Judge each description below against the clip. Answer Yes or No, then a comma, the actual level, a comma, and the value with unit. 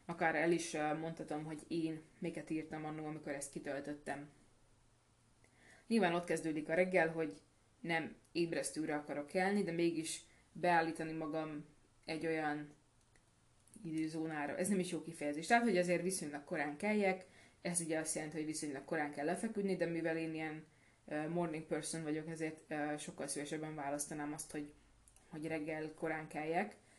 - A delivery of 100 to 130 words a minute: No, average, 145 wpm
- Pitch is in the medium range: Yes, medium, 155 Hz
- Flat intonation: Yes, narrow, 2.1 semitones